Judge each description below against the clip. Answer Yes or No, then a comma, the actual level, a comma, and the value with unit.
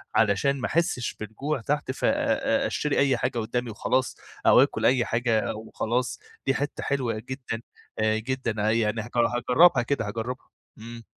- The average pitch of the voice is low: Yes, low, 120 Hz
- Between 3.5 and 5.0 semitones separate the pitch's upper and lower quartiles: No, average, 2.9 semitones